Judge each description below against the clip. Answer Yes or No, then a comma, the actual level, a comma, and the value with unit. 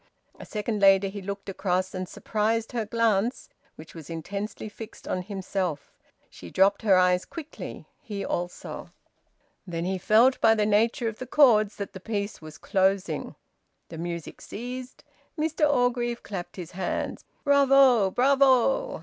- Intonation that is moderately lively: Yes, average, 4.3 semitones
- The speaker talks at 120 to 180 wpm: Yes, average, 150 wpm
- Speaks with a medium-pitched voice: No, high, 205 Hz